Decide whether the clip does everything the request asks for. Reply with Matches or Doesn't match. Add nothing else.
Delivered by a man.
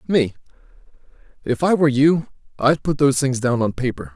Matches